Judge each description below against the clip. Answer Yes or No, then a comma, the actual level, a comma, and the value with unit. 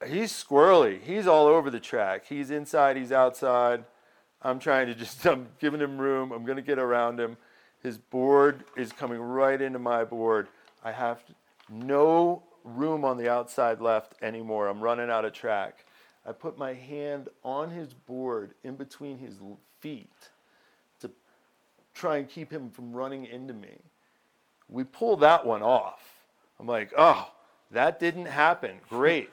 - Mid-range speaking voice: No, low, 130 Hz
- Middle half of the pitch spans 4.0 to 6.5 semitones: No, average, 3.4 semitones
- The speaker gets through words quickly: No, average, 160 wpm